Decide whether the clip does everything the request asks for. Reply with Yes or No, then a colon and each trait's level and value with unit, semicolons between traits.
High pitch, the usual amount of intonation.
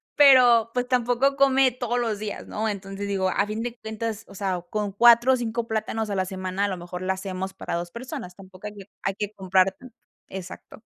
Yes: high, 210 Hz; average, 3.9 semitones